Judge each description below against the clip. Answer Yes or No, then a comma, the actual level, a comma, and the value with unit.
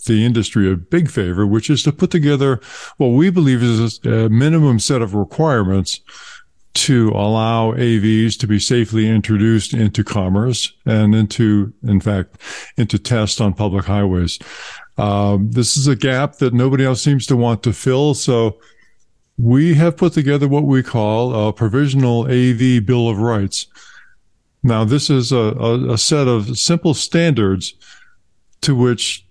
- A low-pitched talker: Yes, low, 120 Hz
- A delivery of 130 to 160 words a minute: Yes, average, 155 wpm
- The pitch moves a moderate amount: Yes, average, 4.3 semitones